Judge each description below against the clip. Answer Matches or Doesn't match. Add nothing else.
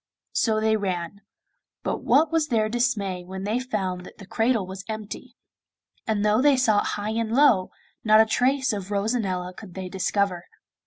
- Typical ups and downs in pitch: Matches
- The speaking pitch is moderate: Doesn't match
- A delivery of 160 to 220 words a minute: Matches